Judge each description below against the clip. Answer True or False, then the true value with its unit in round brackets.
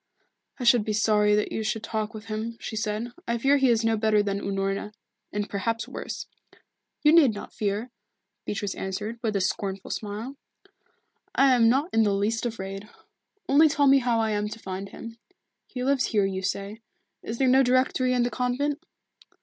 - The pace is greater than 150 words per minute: True (190 wpm)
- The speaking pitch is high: True (225 Hz)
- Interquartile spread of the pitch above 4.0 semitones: False (3.2 semitones)